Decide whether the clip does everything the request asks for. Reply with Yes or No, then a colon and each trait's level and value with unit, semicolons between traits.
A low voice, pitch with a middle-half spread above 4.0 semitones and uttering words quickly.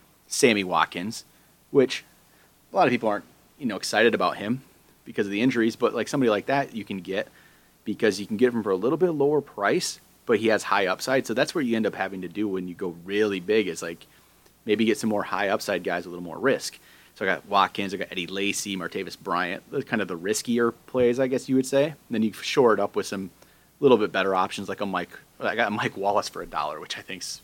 Yes: low, 105 Hz; average, 4.5 semitones; fast, 250 wpm